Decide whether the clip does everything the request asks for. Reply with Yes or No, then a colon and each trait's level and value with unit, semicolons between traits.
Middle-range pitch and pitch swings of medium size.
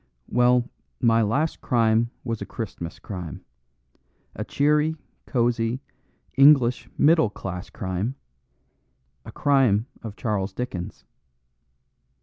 No: low, 115 Hz; average, 4.0 semitones